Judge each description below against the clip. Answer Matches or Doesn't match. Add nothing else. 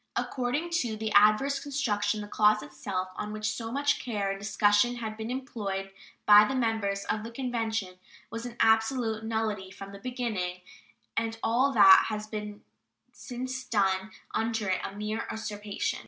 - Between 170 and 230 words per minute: Doesn't match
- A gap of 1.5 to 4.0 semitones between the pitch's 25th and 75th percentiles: Matches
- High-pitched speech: Matches